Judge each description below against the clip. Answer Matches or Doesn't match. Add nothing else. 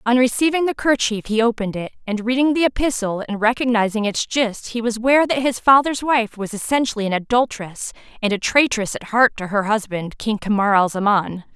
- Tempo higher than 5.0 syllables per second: Matches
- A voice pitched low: Doesn't match